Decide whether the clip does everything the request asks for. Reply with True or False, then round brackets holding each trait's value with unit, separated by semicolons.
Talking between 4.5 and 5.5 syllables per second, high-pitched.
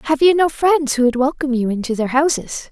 False (5.9 syllables/s; 275 Hz)